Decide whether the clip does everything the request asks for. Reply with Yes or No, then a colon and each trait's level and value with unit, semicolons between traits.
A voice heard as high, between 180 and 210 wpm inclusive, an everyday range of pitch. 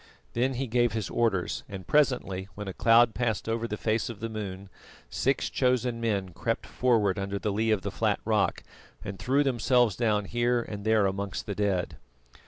No: low, 110 Hz; average, 190 wpm; average, 3.2 semitones